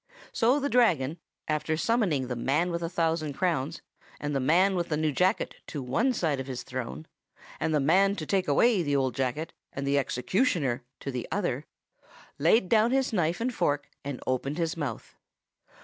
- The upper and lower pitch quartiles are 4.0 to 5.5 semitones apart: Yes, average, 5.2 semitones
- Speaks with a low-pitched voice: No, medium, 155 Hz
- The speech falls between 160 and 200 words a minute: Yes, average, 185 wpm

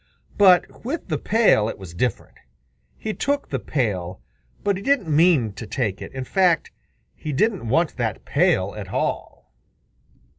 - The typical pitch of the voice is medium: Yes, medium, 150 Hz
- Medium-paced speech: Yes, average, 155 wpm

